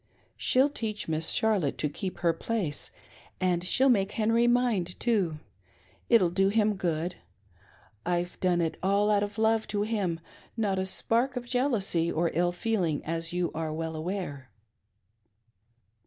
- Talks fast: No, average, 155 wpm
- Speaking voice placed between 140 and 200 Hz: Yes, high, 190 Hz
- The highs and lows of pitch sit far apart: No, average, 4.8 semitones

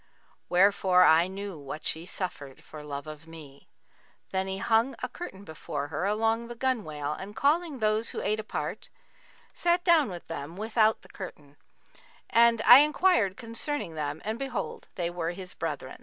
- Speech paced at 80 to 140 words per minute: No, average, 165 wpm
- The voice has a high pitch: Yes, high, 195 Hz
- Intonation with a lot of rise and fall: Yes, wide, 6.1 semitones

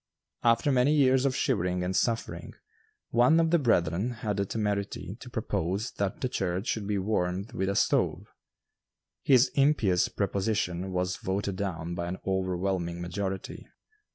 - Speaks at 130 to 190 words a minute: Yes, average, 150 wpm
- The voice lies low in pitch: Yes, low, 100 Hz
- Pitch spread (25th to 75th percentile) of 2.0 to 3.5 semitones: No, average, 4.3 semitones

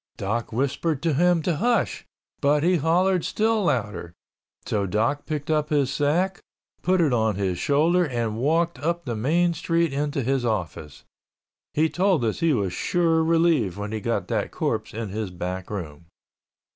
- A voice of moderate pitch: Yes, medium, 145 Hz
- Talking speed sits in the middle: Yes, average, 170 wpm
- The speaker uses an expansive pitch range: Yes, wide, 7.5 semitones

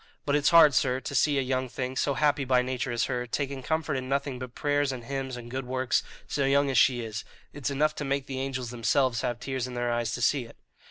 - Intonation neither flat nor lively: No, narrow, 2.2 semitones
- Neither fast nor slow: No, fast, 255 wpm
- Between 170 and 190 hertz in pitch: No, low, 130 Hz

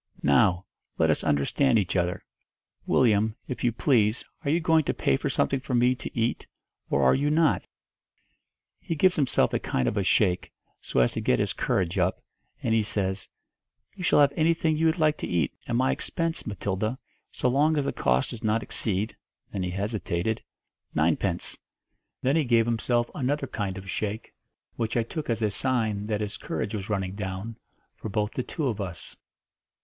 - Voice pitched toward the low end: Yes, low, 110 Hz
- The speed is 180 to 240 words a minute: Yes, average, 185 wpm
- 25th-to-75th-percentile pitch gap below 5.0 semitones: No, wide, 5.5 semitones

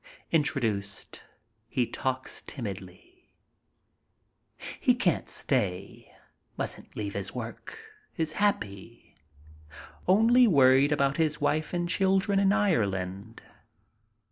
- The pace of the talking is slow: Yes, slow, 90 wpm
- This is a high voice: No, medium, 140 Hz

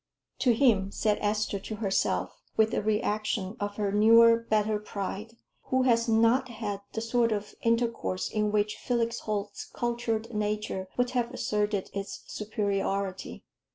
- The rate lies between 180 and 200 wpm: No, average, 145 wpm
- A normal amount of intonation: No, narrow, 2.0 semitones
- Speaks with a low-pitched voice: No, high, 215 Hz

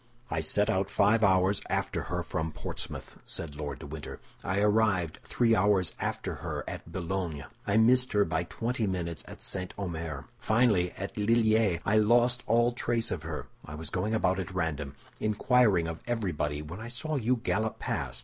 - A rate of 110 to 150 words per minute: No, average, 180 wpm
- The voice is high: No, very low, 95 Hz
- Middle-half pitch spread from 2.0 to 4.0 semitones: No, average, 5.2 semitones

